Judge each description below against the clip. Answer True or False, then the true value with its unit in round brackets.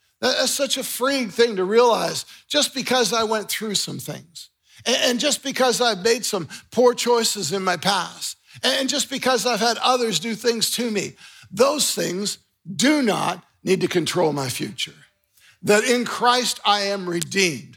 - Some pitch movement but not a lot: True (4.2 semitones)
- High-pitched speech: True (230 Hz)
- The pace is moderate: True (170 wpm)